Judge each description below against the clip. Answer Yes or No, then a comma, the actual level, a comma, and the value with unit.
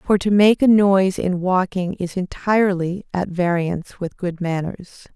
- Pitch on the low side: No, medium, 185 Hz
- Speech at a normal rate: Yes, average, 165 wpm